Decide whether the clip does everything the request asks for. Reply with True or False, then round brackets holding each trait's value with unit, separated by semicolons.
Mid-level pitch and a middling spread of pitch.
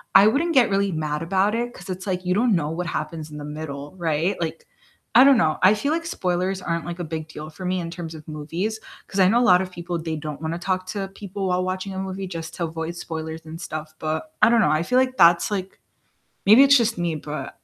True (180 Hz; 3.6 semitones)